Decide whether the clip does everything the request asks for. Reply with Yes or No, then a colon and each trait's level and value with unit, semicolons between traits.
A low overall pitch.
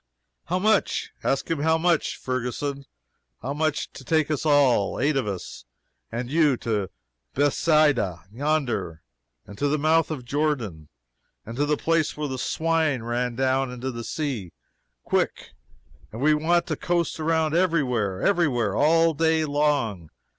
No: medium, 145 Hz